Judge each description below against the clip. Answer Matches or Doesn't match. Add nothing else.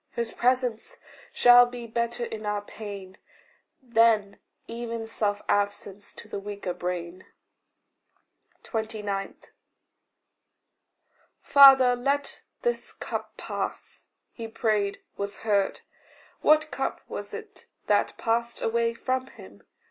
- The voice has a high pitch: Matches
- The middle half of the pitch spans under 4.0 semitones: Matches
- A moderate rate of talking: Doesn't match